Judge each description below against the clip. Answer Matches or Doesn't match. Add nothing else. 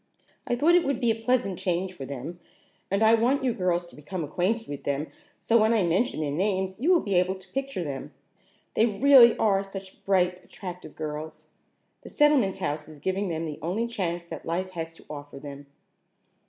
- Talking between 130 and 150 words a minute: Doesn't match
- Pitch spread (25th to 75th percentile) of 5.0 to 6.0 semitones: Matches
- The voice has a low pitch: Doesn't match